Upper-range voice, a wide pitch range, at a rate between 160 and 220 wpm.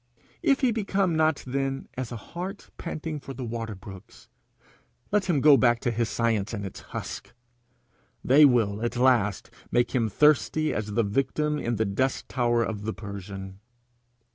No: low, 120 Hz; wide, 5.7 semitones; average, 165 wpm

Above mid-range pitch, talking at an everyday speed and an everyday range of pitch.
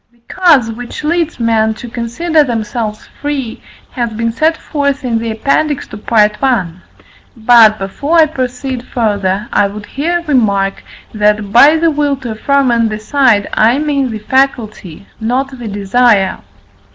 Yes: high, 235 Hz; average, 150 wpm; average, 4.5 semitones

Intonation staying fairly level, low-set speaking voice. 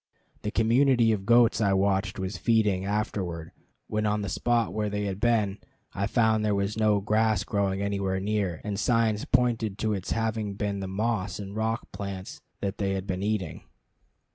Yes: narrow, 2.2 semitones; low, 105 Hz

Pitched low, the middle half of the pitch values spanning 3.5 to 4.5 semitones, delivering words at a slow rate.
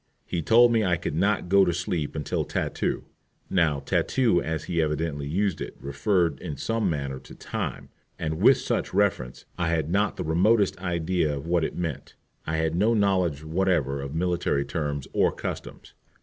No: very low, 85 Hz; average, 4.0 semitones; average, 180 wpm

